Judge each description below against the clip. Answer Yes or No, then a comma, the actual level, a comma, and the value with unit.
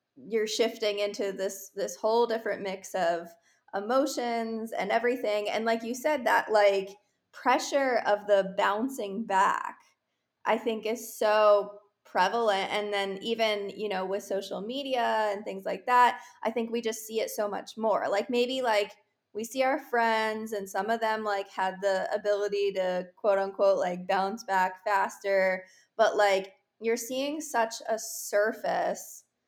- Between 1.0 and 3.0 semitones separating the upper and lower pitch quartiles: Yes, average, 2.7 semitones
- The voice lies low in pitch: No, high, 215 Hz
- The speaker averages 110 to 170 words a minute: Yes, average, 160 wpm